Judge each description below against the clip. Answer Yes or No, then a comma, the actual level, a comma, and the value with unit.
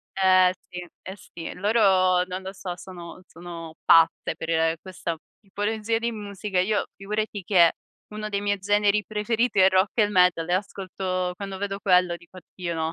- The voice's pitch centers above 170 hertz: Yes, high, 190 Hz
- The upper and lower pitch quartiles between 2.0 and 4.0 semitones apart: Yes, narrow, 2.4 semitones